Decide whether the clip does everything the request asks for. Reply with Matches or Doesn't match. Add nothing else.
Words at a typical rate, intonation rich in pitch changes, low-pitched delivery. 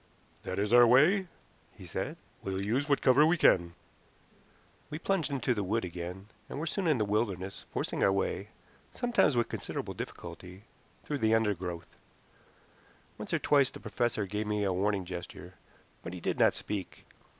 Matches